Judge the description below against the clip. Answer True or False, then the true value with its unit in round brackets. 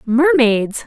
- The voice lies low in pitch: False (250 Hz)